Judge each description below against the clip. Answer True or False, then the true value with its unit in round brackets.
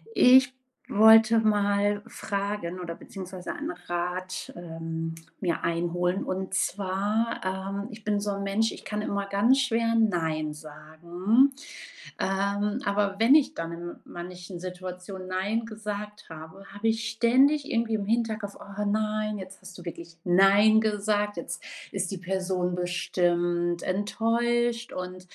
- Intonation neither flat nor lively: True (3.3 semitones)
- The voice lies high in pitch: True (200 Hz)